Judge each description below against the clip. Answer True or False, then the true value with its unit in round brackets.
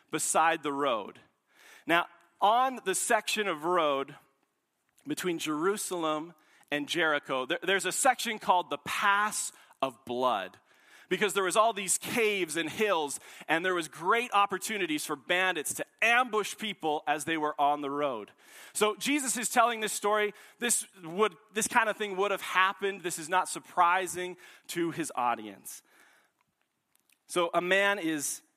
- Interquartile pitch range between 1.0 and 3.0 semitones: False (5.1 semitones)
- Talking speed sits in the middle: True (150 wpm)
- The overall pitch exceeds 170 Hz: True (185 Hz)